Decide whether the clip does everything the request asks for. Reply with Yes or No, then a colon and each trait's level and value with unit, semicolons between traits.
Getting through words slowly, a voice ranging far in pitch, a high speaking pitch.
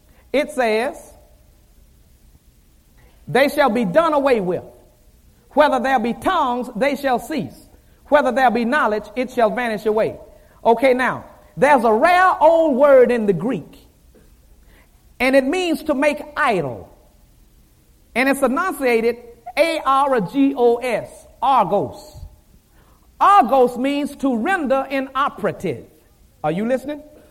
No: slow, 125 wpm; average, 4.3 semitones; very high, 260 Hz